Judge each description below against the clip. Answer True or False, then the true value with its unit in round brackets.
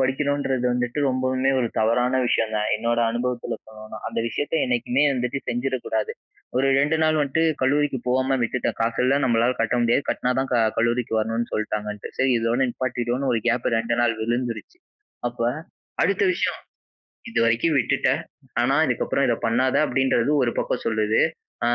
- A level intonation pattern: True (2.3 semitones)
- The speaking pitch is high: False (120 Hz)